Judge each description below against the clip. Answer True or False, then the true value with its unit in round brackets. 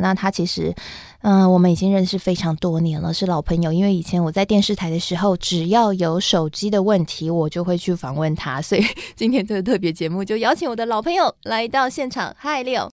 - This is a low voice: False (185 Hz)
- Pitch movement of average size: True (3.8 semitones)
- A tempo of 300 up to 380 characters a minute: True (340 characters per minute)